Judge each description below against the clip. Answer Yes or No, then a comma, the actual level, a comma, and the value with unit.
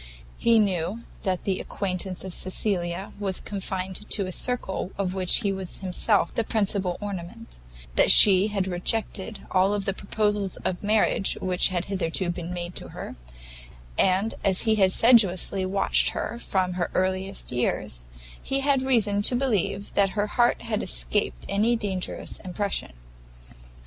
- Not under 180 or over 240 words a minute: No, average, 150 wpm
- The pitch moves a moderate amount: No, narrow, 2.3 semitones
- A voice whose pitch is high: Yes, high, 195 Hz